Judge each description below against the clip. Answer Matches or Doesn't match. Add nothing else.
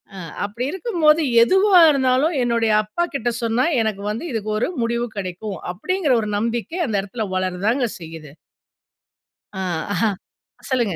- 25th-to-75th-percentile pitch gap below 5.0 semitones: Doesn't match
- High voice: Matches